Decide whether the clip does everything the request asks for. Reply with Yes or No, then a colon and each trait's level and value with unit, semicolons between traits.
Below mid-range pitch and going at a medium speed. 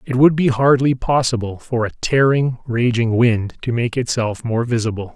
Yes: low, 120 Hz; average, 175 wpm